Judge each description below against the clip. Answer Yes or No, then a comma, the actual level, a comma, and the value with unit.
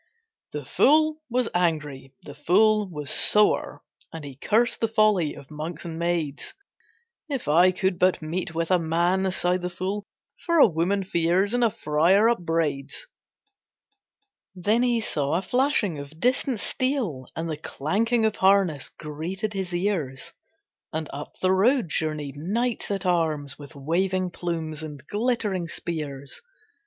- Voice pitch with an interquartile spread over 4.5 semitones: Yes, average, 5.1 semitones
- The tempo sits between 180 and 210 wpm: No, average, 145 wpm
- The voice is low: No, medium, 175 Hz